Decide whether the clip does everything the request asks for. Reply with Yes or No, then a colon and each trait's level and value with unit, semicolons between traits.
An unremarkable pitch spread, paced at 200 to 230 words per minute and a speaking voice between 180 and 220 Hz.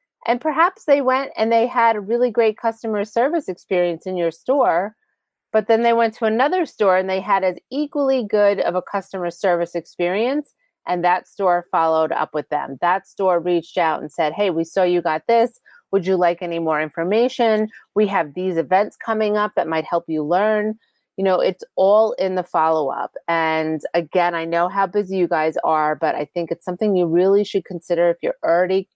Yes: average, 4.5 semitones; fast, 205 wpm; high, 190 Hz